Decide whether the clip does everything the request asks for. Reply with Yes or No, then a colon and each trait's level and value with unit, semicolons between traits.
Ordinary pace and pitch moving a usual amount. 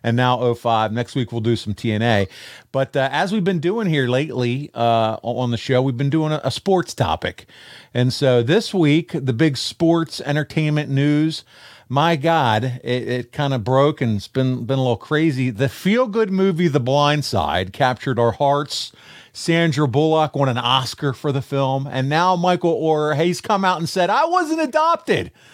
Yes: average, 190 wpm; average, 4.7 semitones